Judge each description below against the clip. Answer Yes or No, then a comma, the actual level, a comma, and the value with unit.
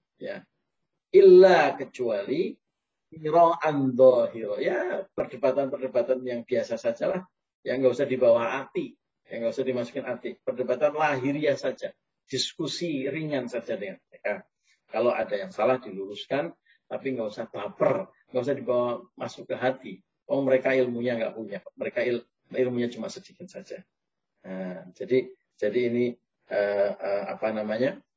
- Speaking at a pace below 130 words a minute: No, average, 135 wpm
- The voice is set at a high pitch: No, low, 130 Hz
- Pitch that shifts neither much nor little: No, wide, 6.6 semitones